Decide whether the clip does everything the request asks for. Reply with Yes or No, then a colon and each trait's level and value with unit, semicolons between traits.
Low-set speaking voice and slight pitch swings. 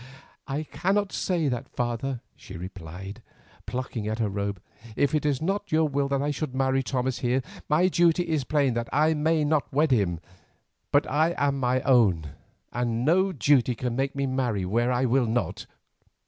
No: low, 130 Hz; average, 4.2 semitones